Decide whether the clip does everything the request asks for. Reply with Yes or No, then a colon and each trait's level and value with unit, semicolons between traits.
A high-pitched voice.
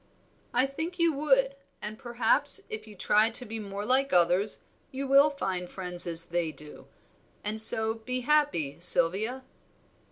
Yes: high, 220 Hz